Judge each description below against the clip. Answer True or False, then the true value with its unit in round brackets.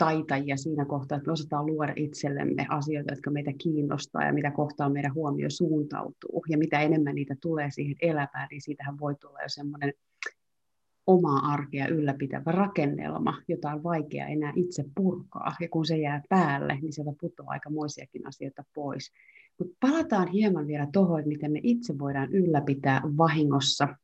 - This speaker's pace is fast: True (160 wpm)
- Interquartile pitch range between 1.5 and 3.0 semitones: True (2.4 semitones)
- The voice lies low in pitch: False (150 Hz)